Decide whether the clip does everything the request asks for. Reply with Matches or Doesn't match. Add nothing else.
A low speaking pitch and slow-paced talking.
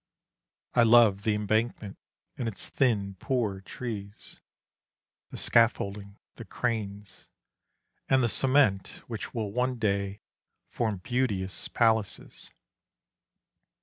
Matches